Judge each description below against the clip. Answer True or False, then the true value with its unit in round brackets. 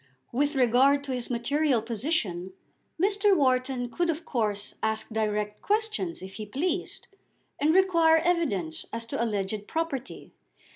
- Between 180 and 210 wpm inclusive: False (135 wpm)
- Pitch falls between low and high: False (255 Hz)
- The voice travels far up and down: True (6.9 semitones)